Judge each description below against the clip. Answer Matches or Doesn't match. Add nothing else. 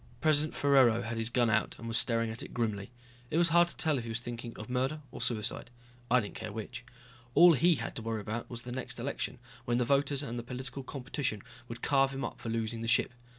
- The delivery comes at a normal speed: Doesn't match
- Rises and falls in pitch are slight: Doesn't match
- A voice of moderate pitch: Doesn't match